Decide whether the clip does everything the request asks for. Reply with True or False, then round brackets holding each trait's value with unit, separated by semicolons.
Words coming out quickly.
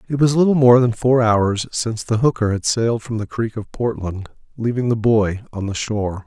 True (220 wpm)